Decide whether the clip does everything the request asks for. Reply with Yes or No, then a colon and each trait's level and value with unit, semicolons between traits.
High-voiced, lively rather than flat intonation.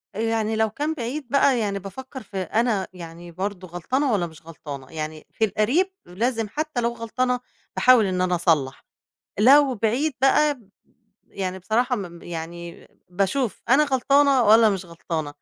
Yes: high, 220 Hz; wide, 6.2 semitones